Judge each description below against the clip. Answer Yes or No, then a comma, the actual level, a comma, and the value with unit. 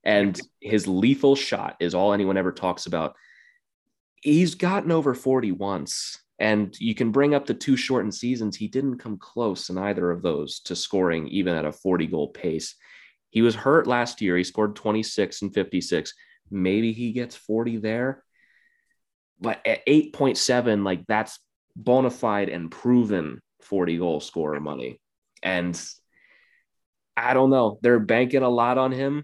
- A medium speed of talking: Yes, average, 160 wpm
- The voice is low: Yes, low, 115 Hz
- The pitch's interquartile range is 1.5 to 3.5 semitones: No, average, 5.2 semitones